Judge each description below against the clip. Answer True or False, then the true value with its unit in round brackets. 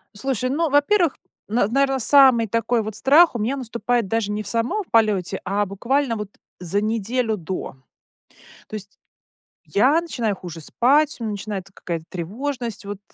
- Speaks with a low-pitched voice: False (230 Hz)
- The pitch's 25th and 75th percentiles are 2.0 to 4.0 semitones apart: False (4.8 semitones)